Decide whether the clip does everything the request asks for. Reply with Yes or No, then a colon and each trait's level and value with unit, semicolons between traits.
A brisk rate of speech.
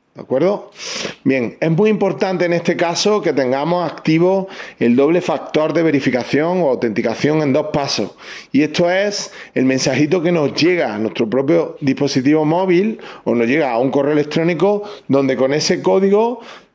No: average, 165 wpm